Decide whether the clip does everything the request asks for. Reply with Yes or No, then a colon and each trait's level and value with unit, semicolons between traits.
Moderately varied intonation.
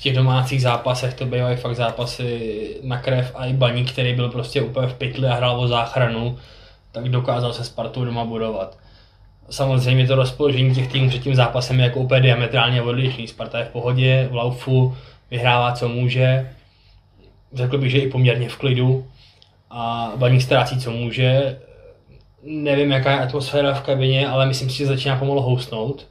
No: narrow, 1.9 semitones